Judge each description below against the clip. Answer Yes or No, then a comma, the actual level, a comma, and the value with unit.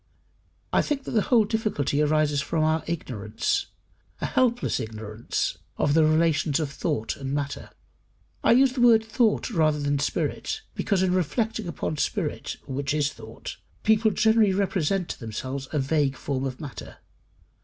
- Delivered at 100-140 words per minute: No, average, 155 wpm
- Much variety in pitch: Yes, wide, 7.1 semitones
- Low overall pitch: No, medium, 155 Hz